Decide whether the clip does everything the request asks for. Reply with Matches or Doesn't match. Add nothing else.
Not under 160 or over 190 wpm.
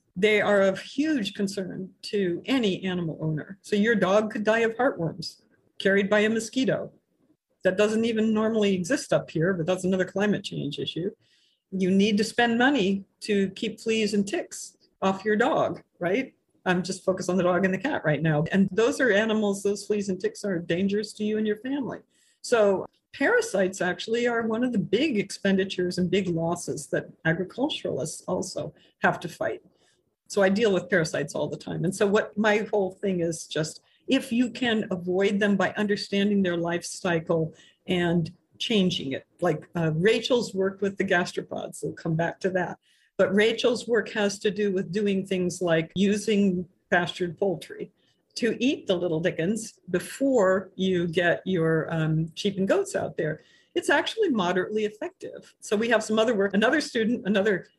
Matches